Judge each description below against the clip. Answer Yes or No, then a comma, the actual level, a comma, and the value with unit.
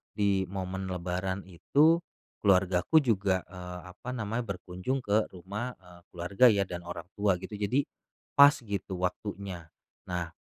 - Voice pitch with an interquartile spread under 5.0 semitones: Yes, average, 2.7 semitones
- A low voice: Yes, very low, 95 Hz